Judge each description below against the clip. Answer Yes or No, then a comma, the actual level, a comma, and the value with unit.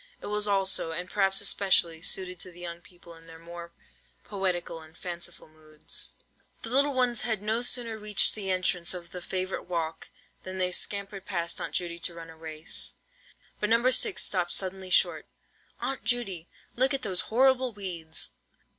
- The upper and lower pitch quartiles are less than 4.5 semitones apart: Yes, average, 3.6 semitones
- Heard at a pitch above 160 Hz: Yes, medium, 185 Hz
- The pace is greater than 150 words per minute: Yes, average, 175 wpm